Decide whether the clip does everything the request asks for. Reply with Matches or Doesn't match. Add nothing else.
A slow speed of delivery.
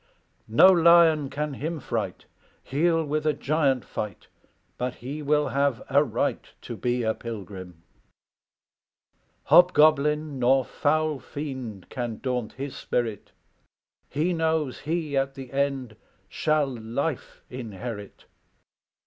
Matches